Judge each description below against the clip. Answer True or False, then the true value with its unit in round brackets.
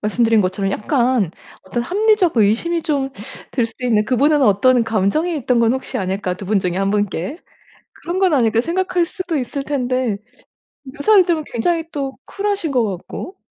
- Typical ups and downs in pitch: False (7.4 semitones)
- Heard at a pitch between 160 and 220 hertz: False (255 Hz)